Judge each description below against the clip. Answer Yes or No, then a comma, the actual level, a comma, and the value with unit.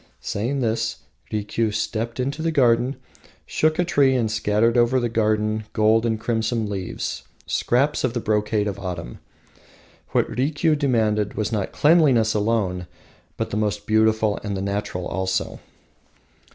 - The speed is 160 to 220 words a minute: No, average, 140 wpm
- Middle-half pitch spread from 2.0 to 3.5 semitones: Yes, average, 2.9 semitones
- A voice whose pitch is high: No, low, 110 Hz